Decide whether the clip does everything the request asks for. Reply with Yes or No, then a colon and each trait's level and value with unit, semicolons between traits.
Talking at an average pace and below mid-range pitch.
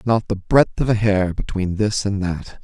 No: fast, 230 wpm; low, 100 Hz